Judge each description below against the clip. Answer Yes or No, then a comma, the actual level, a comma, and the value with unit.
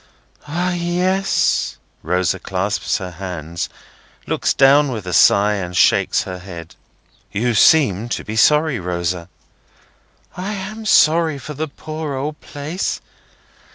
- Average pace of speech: No, slow, 125 wpm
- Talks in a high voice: No, low, 130 Hz